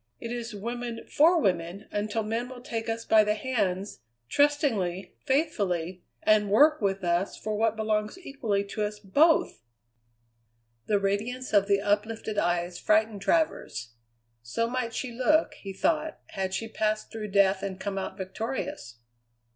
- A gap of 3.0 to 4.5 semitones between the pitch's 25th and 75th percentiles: Yes, average, 3.5 semitones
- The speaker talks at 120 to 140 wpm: No, average, 150 wpm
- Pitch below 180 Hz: No, high, 215 Hz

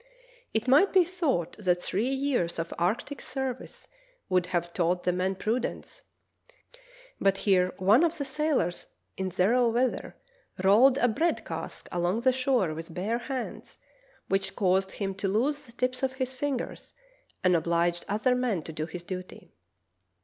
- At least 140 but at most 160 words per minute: Yes, average, 155 wpm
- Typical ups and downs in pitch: No, wide, 6.2 semitones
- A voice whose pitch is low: No, high, 210 Hz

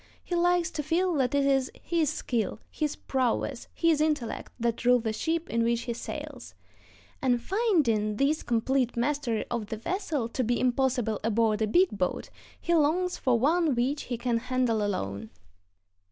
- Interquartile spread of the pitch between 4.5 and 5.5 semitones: Yes, average, 4.9 semitones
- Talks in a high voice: Yes, very high, 255 Hz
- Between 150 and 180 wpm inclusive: Yes, average, 170 wpm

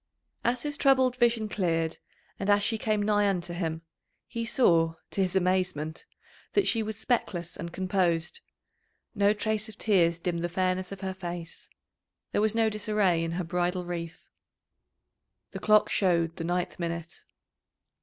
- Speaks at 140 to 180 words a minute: Yes, average, 155 wpm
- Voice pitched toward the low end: No, medium, 185 Hz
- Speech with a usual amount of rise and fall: Yes, average, 3.8 semitones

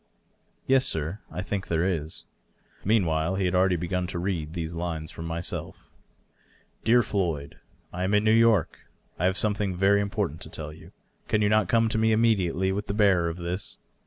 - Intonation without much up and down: No, average, 3.7 semitones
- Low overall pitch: Yes, very low, 95 Hz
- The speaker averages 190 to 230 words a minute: Yes, fast, 205 wpm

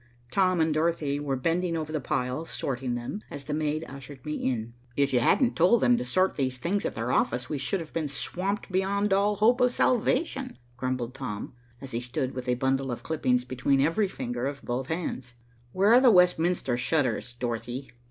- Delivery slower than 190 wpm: No, average, 200 wpm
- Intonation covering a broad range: Yes, wide, 6.2 semitones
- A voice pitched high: No, medium, 145 Hz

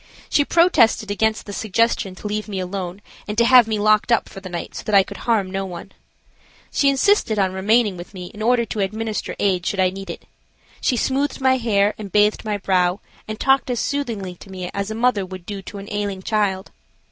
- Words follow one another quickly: Yes, fast, 220 wpm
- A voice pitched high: Yes, high, 210 Hz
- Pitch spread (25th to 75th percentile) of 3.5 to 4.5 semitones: No, average, 3.0 semitones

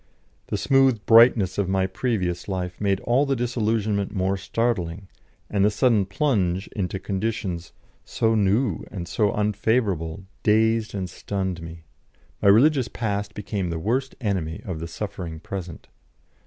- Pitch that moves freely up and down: No, average, 3.5 semitones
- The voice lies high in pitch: No, low, 100 Hz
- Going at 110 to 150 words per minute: Yes, average, 140 wpm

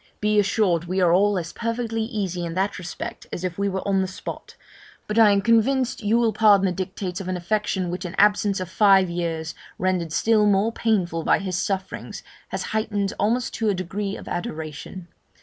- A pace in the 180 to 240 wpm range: Yes, average, 200 wpm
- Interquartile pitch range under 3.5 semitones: Yes, average, 2.8 semitones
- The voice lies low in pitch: No, high, 195 Hz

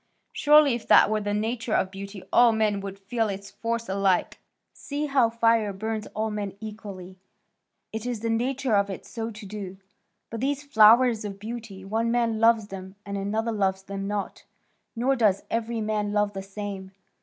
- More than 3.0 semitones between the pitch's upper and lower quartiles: No, narrow, 2.6 semitones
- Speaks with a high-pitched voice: Yes, high, 215 Hz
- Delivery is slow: No, average, 180 wpm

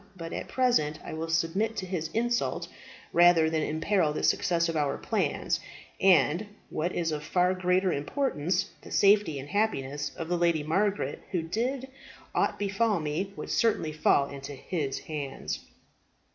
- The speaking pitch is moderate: Yes, medium, 170 Hz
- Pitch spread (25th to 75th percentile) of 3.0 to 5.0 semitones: Yes, average, 4.3 semitones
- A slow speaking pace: No, average, 160 wpm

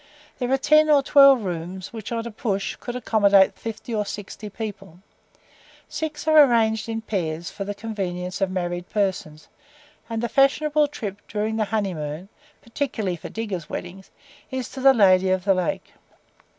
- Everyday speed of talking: Yes, average, 165 wpm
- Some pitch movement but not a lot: Yes, average, 4.2 semitones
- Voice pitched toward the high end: Yes, high, 210 Hz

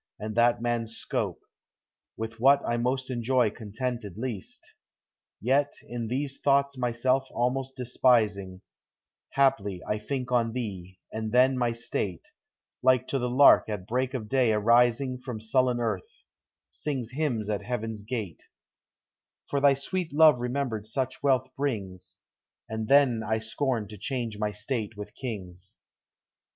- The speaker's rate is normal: Yes, average, 150 wpm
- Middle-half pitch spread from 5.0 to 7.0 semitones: No, average, 3.2 semitones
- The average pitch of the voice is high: No, low, 120 Hz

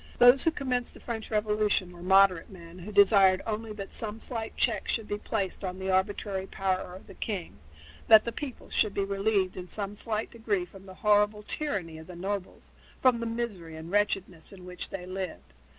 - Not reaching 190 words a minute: No, average, 200 wpm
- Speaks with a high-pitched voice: Yes, high, 200 Hz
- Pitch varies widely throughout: No, average, 2.9 semitones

